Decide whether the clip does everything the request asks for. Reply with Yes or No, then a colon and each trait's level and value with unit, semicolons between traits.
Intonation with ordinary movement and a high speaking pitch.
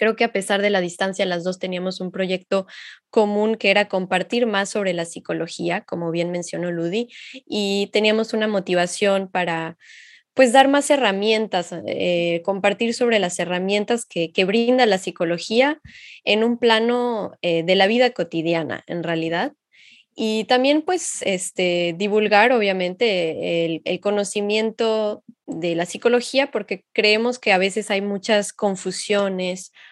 Yes: average, 3.9 semitones; high, 200 Hz